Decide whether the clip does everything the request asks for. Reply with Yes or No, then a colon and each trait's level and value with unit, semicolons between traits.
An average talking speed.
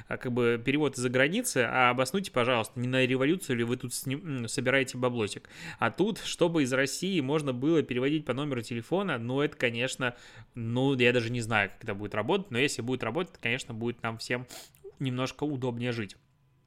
No: fast, 185 wpm